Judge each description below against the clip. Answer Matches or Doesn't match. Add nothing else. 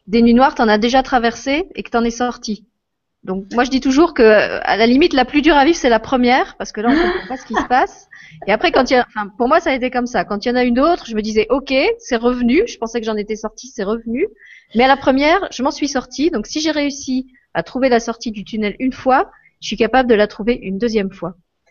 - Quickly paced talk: Matches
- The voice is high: Matches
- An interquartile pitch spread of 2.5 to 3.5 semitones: Doesn't match